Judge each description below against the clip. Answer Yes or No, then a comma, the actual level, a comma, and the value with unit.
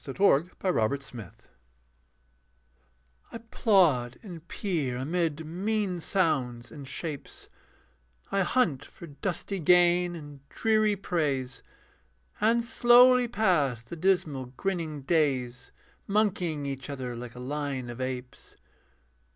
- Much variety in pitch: Yes, wide, 6.6 semitones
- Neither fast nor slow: No, slow, 110 wpm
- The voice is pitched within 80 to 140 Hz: No, medium, 160 Hz